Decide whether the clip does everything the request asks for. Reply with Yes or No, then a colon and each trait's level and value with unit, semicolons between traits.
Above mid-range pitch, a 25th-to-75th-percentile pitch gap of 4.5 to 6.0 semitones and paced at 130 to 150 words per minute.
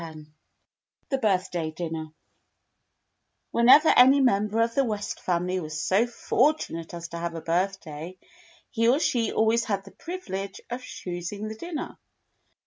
Yes: high, 200 Hz; wide, 5.5 semitones; average, 140 wpm